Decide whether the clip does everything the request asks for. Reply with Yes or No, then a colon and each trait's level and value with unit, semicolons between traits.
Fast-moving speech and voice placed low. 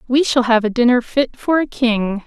No: fast, 240 wpm; high, 240 Hz